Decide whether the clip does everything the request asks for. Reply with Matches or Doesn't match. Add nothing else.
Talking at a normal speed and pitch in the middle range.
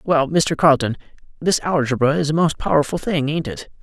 Matches